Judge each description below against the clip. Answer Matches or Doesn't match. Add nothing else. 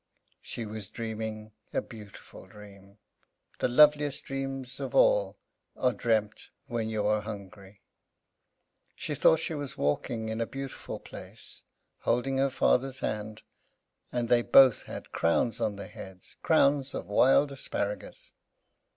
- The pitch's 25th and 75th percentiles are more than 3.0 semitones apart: Matches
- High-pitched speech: Doesn't match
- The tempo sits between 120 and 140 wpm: Matches